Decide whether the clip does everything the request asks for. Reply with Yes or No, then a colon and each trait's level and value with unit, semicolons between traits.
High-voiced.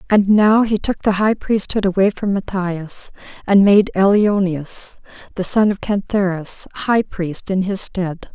Yes: high, 195 Hz